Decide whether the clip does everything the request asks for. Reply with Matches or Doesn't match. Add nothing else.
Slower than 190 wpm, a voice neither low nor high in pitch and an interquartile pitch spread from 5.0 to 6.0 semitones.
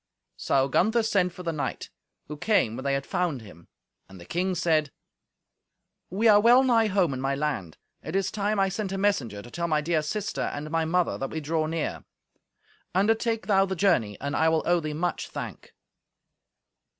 Doesn't match